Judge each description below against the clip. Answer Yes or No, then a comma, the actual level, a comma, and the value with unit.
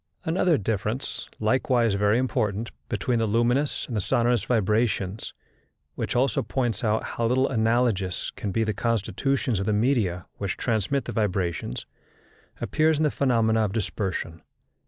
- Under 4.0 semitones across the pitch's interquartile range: Yes, average, 3.3 semitones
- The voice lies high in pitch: No, low, 115 Hz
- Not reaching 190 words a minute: Yes, average, 145 wpm